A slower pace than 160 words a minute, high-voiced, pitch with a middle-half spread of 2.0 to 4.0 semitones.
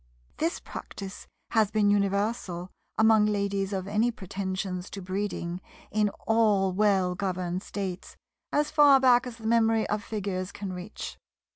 Yes: average, 140 wpm; high, 205 Hz; average, 2.7 semitones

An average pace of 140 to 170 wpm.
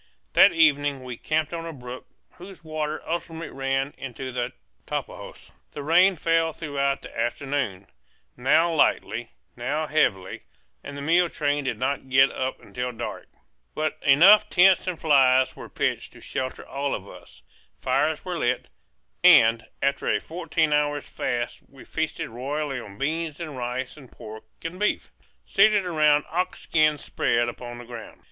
Yes: average, 155 wpm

